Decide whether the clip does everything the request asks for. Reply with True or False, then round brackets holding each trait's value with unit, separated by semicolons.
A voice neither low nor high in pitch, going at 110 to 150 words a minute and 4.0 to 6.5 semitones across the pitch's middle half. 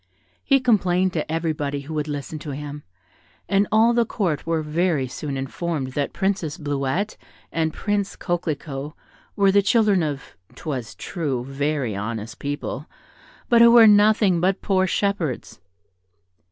True (160 Hz; 140 wpm; 5.6 semitones)